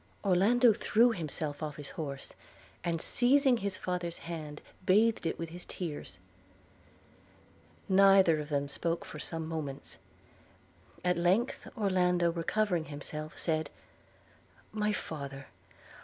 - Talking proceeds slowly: Yes, slow, 115 wpm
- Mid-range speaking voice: Yes, medium, 170 Hz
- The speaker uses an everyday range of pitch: Yes, average, 4.2 semitones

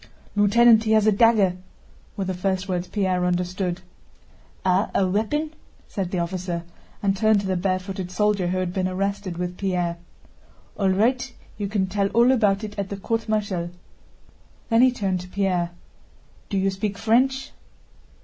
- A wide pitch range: No, average, 2.7 semitones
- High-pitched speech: Yes, high, 195 Hz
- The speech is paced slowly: No, average, 165 wpm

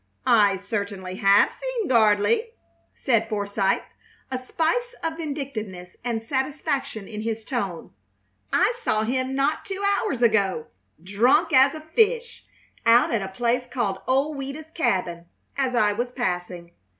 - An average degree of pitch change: No, wide, 6.0 semitones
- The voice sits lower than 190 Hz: No, high, 240 Hz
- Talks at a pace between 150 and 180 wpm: No, average, 140 wpm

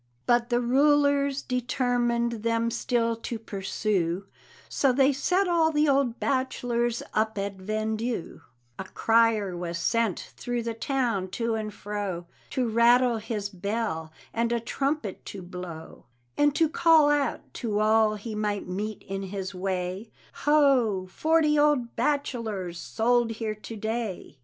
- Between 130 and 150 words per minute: Yes, average, 140 wpm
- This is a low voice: No, high, 230 Hz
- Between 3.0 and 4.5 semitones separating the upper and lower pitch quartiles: Yes, average, 3.8 semitones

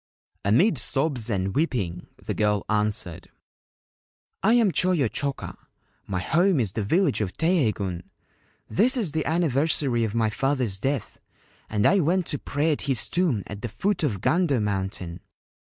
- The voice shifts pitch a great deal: Yes, wide, 7.8 semitones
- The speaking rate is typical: Yes, average, 155 wpm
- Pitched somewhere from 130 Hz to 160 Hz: Yes, low, 135 Hz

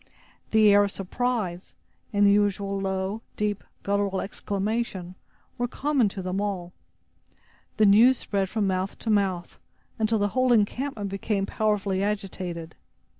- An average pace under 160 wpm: Yes, slow, 135 wpm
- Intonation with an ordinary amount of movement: No, narrow, 2.1 semitones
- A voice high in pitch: Yes, high, 200 Hz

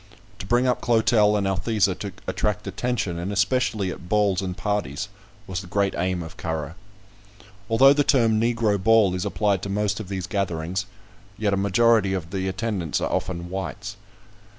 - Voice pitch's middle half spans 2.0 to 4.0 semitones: Yes, average, 2.9 semitones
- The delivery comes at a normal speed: Yes, average, 175 wpm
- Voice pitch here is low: Yes, low, 100 Hz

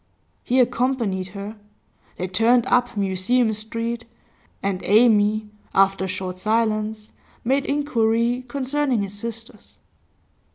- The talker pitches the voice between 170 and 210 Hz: No, high, 225 Hz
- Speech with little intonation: No, average, 3.3 semitones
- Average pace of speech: No, slow, 110 wpm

